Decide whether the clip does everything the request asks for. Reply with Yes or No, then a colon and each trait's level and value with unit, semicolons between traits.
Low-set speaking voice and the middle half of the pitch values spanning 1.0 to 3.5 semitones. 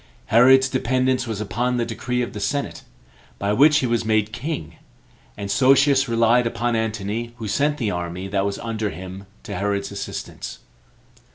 No: low, 115 Hz; average, 3.9 semitones